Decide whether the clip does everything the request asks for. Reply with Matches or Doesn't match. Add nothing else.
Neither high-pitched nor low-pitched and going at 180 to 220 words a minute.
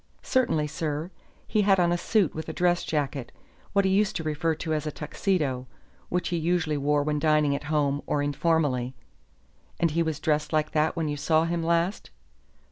Matches